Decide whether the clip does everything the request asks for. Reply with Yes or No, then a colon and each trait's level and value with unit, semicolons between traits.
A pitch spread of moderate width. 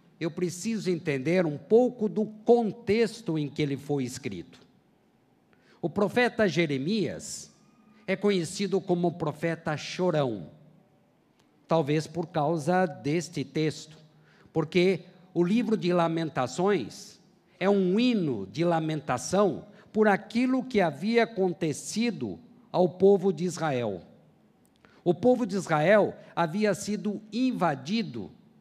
Yes: average, 4.6 semitones